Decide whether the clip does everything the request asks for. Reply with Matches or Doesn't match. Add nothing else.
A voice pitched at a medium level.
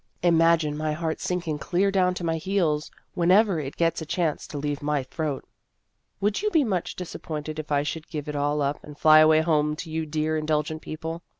Matches